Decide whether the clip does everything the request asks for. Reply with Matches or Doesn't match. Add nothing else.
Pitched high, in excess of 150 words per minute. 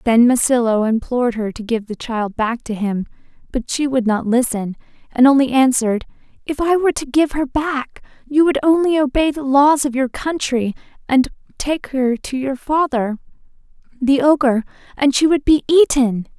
Matches